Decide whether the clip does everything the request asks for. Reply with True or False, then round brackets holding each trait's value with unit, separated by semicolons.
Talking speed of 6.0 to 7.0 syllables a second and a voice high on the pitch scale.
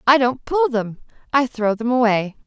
False (4.7 syllables/s; 245 Hz)